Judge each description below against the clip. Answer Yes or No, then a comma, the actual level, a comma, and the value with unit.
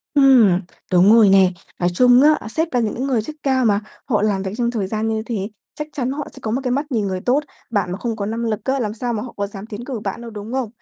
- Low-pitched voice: No, high, 225 Hz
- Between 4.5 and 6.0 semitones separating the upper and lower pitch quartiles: No, average, 3.7 semitones